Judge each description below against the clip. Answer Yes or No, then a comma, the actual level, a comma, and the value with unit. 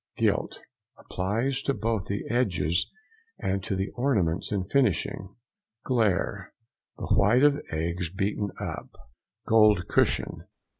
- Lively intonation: No, average, 4.0 semitones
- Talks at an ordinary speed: No, slow, 105 wpm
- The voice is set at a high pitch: No, low, 100 Hz